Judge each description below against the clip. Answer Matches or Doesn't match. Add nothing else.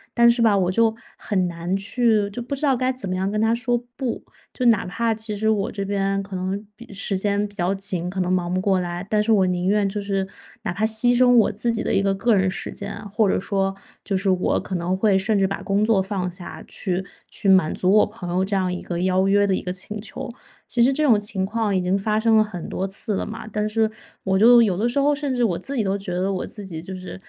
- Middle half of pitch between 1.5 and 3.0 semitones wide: Matches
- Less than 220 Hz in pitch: Matches